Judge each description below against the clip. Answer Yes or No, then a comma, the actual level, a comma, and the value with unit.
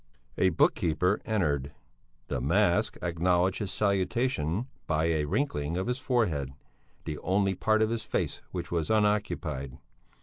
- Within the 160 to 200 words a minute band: No, average, 140 wpm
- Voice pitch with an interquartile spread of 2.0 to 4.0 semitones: No, average, 5.3 semitones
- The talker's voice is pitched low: Yes, very low, 90 Hz